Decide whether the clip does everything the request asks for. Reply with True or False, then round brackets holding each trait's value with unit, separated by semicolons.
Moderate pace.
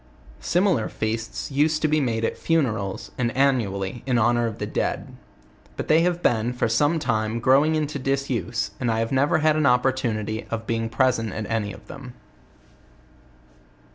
True (165 wpm)